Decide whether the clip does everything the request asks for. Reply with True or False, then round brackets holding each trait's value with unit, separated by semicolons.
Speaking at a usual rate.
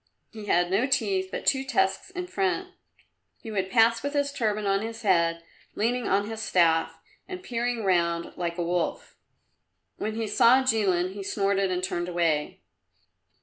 True (165 wpm)